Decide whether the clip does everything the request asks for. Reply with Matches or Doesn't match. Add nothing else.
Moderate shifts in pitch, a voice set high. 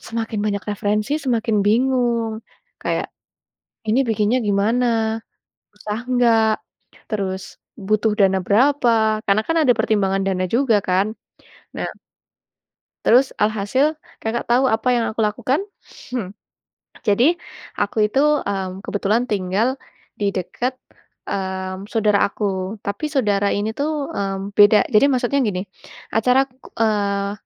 Matches